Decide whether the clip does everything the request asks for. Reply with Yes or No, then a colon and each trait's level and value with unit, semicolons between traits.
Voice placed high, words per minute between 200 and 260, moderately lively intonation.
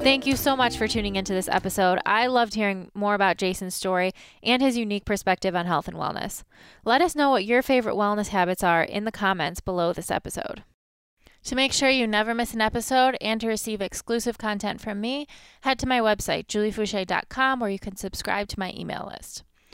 Yes: high, 210 Hz; fast, 205 wpm; average, 4.2 semitones